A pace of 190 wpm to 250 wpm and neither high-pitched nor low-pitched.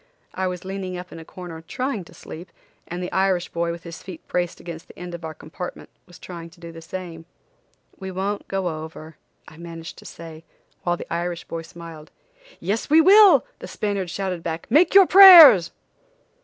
Yes: average, 195 wpm; medium, 175 Hz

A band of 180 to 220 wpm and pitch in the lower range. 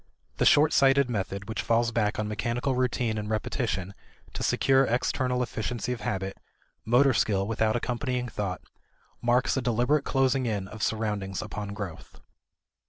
No: average, 150 wpm; low, 115 Hz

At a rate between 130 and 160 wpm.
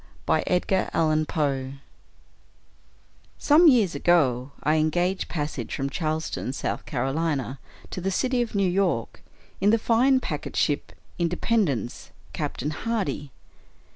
Yes: average, 140 wpm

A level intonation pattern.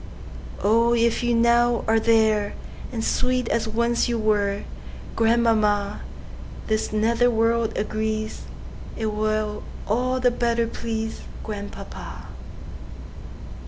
Yes: narrow, 1.5 semitones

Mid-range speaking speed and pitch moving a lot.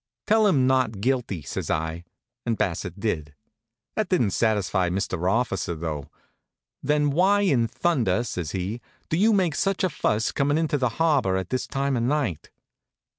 Yes: average, 165 wpm; wide, 8.0 semitones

